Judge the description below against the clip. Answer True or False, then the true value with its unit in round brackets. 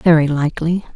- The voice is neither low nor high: True (160 Hz)